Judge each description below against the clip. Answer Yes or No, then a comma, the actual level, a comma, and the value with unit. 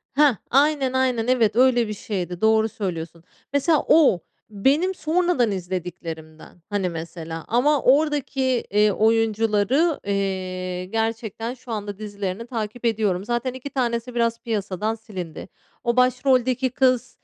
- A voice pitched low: No, high, 225 Hz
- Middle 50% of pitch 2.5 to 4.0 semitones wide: No, average, 4.6 semitones